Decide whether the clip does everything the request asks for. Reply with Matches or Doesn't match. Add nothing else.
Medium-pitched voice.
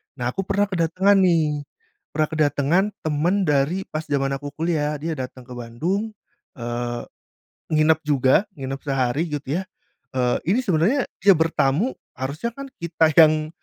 Matches